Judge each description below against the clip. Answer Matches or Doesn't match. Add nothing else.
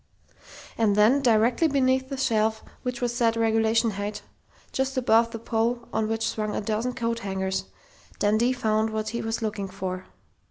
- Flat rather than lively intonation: Matches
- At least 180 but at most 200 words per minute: Doesn't match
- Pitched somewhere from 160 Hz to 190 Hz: Doesn't match